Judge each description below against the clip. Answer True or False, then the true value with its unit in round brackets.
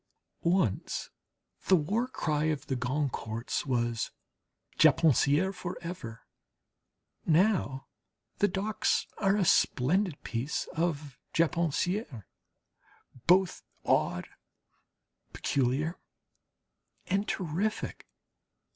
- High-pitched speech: False (160 Hz)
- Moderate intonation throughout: False (6.1 semitones)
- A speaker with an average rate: False (80 wpm)